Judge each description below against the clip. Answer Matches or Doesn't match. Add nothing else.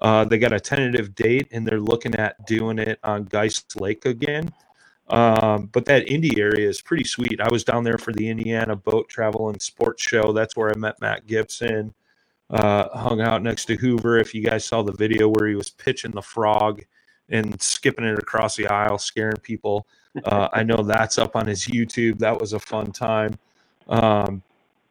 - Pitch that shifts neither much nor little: Doesn't match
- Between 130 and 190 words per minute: Doesn't match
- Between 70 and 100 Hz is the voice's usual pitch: Doesn't match